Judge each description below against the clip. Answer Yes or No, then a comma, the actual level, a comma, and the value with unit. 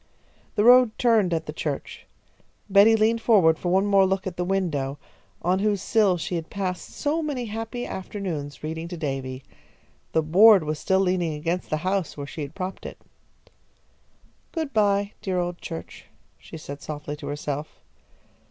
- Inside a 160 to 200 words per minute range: Yes, average, 170 wpm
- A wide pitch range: No, average, 4.7 semitones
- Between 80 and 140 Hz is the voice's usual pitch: No, medium, 185 Hz